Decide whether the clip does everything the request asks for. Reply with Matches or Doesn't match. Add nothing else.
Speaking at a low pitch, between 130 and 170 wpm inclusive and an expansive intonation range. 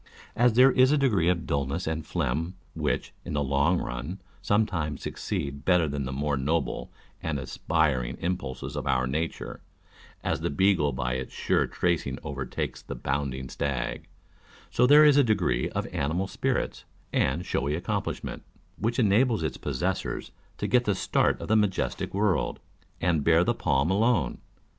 Matches